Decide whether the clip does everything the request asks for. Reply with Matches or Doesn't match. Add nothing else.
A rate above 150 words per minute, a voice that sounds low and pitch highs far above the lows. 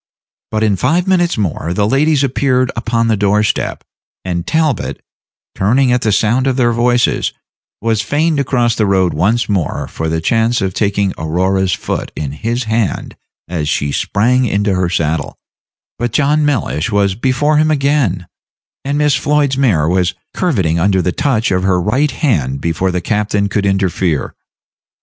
Matches